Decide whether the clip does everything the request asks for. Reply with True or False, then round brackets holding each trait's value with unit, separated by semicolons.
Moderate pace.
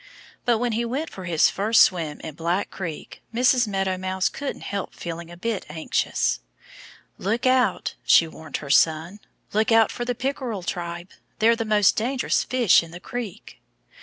True (170 wpm)